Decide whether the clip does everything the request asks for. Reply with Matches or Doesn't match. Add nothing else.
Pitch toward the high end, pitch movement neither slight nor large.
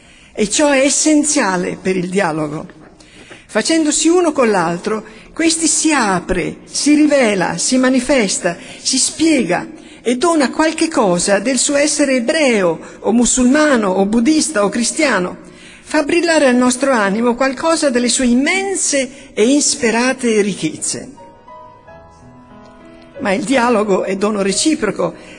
Doesn't match